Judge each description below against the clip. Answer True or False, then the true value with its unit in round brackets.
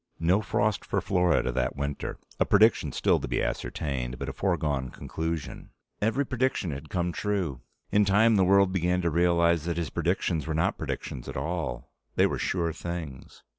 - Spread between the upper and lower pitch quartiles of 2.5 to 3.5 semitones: False (4.5 semitones)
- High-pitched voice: False (85 Hz)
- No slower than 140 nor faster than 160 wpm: False (175 wpm)